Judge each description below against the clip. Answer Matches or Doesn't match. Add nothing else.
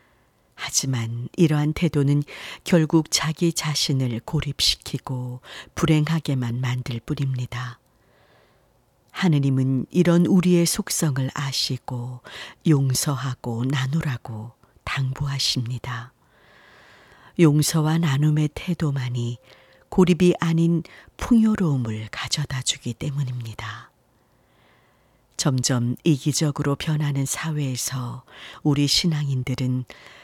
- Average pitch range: Matches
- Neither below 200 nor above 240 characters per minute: Matches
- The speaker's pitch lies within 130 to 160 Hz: Matches